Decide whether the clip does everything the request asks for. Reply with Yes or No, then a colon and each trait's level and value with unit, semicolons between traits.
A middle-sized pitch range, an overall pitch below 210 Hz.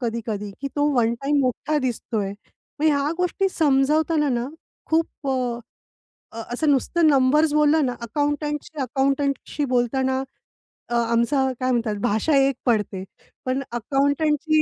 No: average, 3.8 semitones; very high, 275 Hz